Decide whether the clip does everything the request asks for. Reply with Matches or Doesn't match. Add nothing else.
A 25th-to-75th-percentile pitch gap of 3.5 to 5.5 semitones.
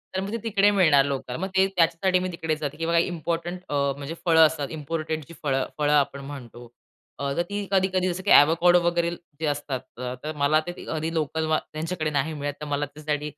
Doesn't match